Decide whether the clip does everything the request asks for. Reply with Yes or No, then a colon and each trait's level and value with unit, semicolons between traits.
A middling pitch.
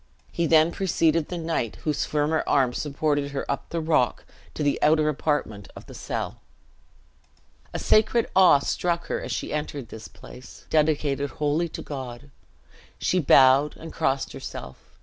Yes: medium, 150 Hz